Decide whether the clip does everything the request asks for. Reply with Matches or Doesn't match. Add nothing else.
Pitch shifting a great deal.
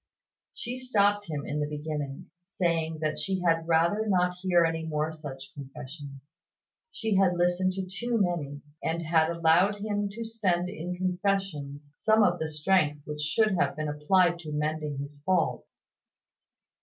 Doesn't match